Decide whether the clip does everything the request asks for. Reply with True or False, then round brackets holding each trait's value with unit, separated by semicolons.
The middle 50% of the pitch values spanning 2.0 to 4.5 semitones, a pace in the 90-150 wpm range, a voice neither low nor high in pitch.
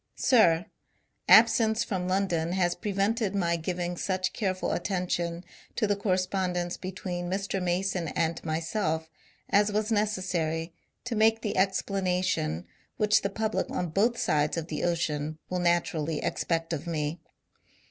True (3.1 semitones; 140 wpm; 180 Hz)